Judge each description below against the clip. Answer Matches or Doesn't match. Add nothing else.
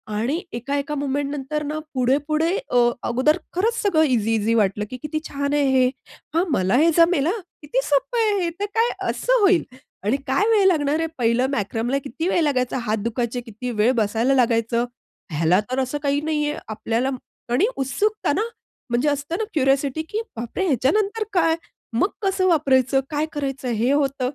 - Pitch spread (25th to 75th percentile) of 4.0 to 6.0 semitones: Matches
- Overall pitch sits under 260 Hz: Doesn't match